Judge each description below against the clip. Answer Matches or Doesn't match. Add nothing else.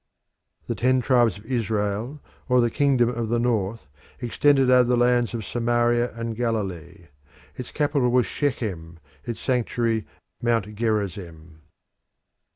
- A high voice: Doesn't match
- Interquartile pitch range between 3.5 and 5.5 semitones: Doesn't match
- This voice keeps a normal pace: Doesn't match